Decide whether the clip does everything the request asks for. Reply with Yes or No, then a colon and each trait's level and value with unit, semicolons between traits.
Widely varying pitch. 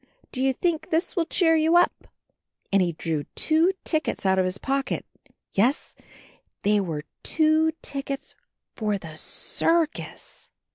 Yes: wide, 8.7 semitones